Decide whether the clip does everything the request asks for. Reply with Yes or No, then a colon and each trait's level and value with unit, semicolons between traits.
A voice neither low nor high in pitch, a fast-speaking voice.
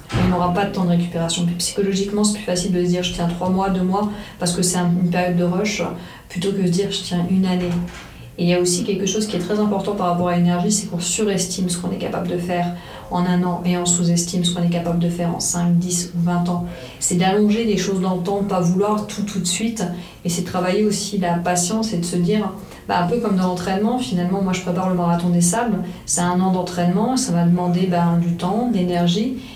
Yes: medium, 180 Hz; fast, 260 wpm